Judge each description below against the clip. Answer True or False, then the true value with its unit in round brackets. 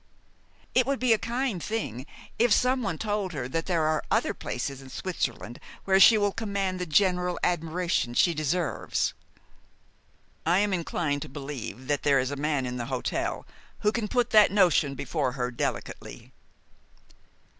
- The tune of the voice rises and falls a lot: True (6.5 semitones)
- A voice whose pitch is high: False (175 Hz)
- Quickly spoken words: False (160 wpm)